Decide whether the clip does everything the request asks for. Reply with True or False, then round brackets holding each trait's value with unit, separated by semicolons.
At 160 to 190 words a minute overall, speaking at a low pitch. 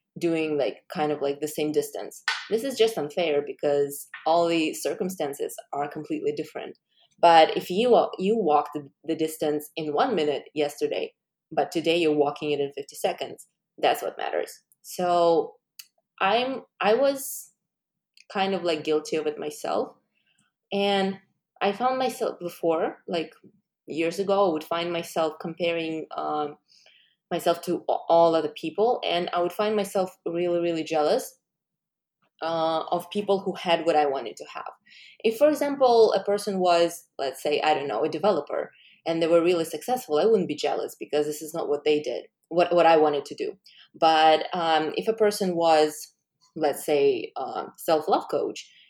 False (170 wpm; 170 Hz)